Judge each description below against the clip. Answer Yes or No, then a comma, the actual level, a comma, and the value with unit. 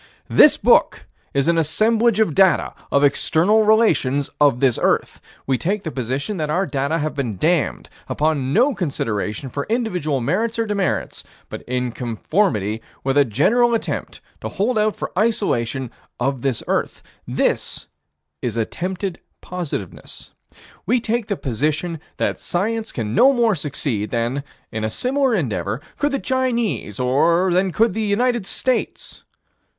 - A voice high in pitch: No, medium, 165 Hz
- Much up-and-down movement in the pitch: Yes, wide, 8.6 semitones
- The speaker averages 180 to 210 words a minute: No, average, 150 wpm